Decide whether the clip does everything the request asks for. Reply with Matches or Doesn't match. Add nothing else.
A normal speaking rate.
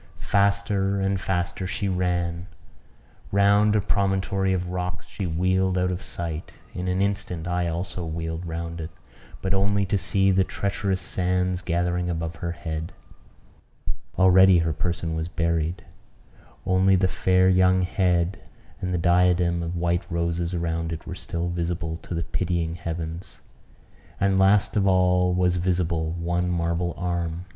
Matches